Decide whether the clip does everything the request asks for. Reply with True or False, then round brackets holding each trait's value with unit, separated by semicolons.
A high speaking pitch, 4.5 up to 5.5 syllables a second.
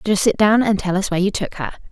False (200 Hz; 6.9 syllables/s)